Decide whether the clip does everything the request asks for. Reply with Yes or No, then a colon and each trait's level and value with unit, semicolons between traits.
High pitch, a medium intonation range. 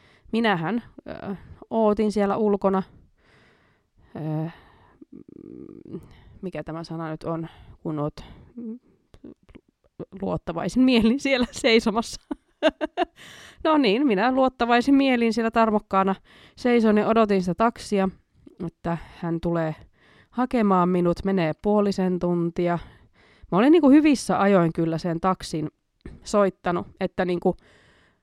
No: high, 195 Hz; wide, 5.7 semitones